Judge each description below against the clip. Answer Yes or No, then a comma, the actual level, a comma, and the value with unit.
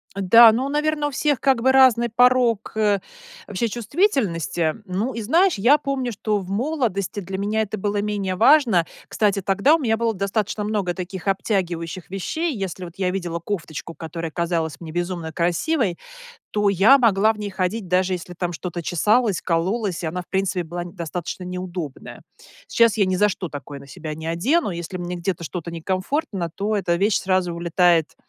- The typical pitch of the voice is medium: No, high, 195 Hz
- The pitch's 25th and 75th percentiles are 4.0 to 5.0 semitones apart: Yes, average, 4.6 semitones